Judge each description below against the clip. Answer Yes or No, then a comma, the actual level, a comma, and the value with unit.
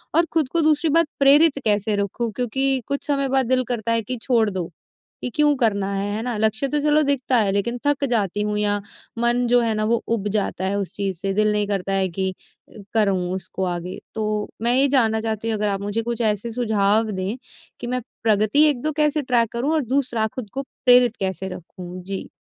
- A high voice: Yes, high, 225 Hz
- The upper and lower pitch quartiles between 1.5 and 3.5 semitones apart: No, average, 4.4 semitones